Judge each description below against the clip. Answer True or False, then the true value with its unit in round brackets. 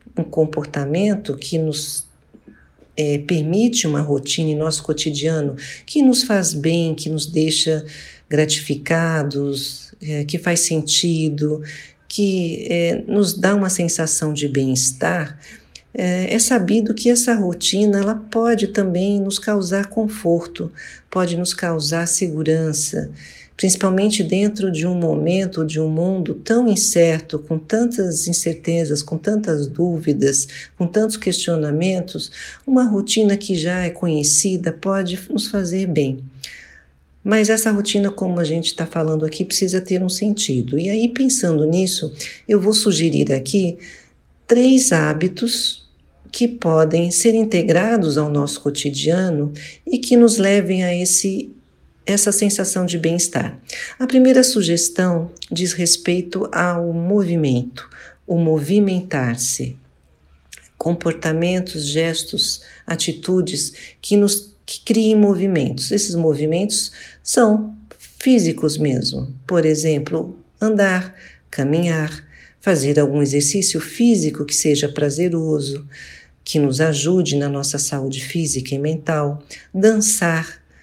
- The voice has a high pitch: False (170 Hz)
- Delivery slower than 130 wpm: True (120 wpm)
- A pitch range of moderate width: True (4.6 semitones)